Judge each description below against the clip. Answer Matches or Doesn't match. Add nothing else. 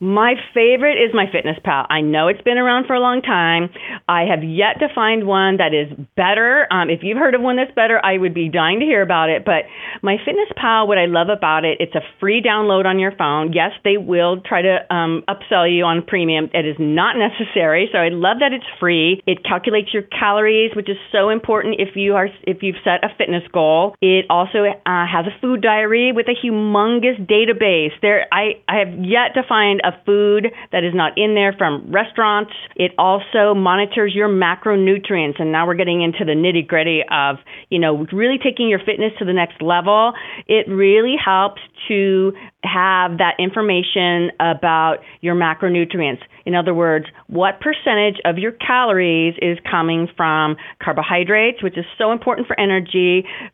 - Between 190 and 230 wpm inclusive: Matches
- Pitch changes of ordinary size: Matches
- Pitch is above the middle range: Matches